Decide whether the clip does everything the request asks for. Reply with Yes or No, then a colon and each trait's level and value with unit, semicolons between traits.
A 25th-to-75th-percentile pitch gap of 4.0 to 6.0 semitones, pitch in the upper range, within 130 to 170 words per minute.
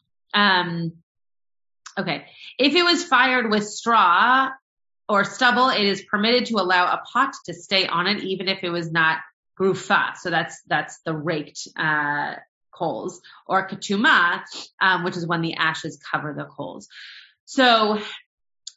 Yes: average, 5.2 semitones; high, 195 Hz; average, 145 wpm